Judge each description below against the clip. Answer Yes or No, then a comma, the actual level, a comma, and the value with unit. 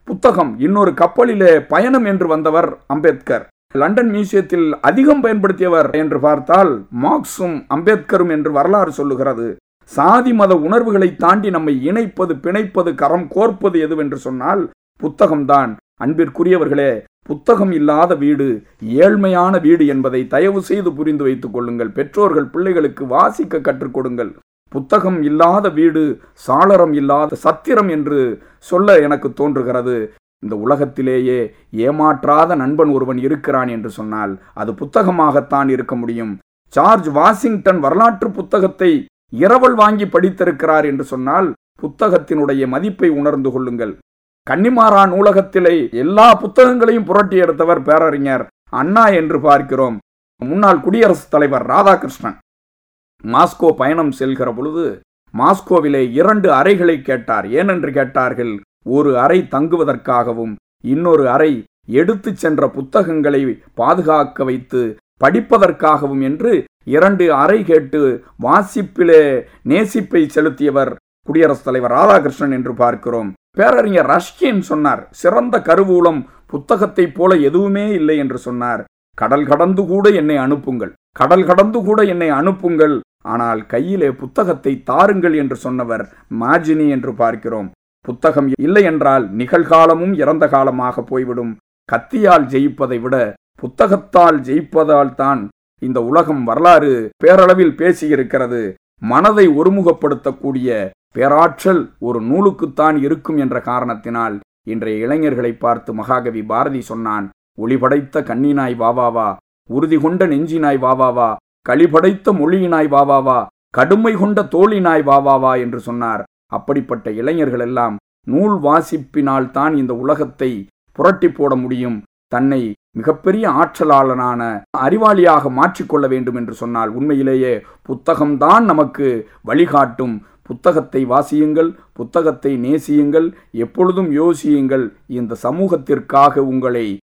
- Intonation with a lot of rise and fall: Yes, wide, 5.9 semitones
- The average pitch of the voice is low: No, medium, 150 Hz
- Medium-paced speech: No, slow, 105 wpm